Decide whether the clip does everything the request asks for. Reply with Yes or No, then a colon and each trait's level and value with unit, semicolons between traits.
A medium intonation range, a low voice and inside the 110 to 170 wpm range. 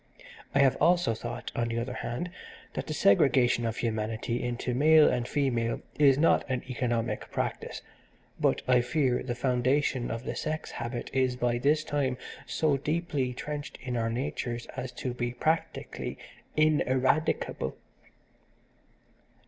Yes: average, 3.3 semitones; low, 125 Hz; average, 140 wpm